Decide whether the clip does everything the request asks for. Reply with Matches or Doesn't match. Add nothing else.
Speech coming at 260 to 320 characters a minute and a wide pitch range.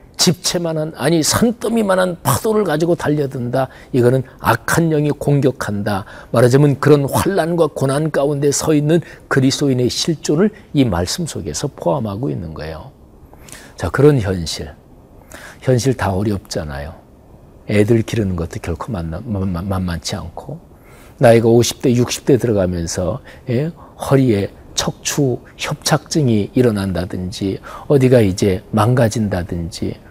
Matches